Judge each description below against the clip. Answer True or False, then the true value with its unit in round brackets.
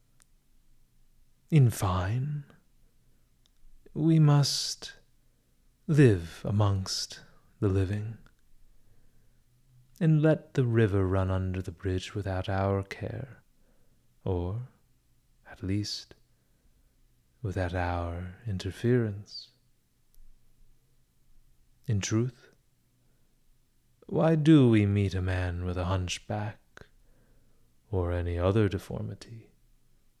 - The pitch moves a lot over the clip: False (4.8 semitones)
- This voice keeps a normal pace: False (80 wpm)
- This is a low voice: True (105 Hz)